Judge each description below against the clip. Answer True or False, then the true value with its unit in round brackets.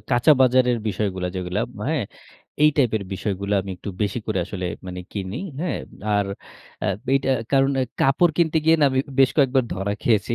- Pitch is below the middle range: True (115 Hz)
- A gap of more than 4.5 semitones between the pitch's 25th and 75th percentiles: True (5.5 semitones)